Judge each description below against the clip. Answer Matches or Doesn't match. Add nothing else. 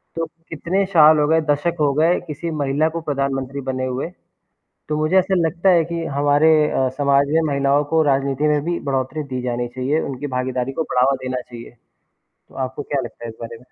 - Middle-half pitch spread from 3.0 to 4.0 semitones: Matches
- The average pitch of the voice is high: Doesn't match